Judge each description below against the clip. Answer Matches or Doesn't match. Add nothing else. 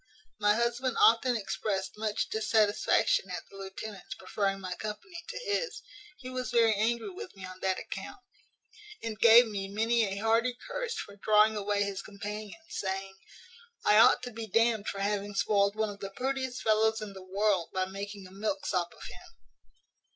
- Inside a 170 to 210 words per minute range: Matches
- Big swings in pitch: Doesn't match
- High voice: Matches